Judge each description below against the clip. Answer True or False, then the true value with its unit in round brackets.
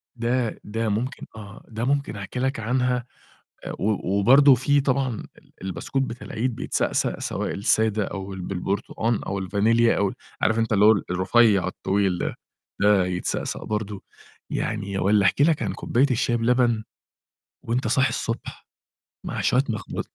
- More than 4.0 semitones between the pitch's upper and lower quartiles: False (3.7 semitones)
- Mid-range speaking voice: False (110 Hz)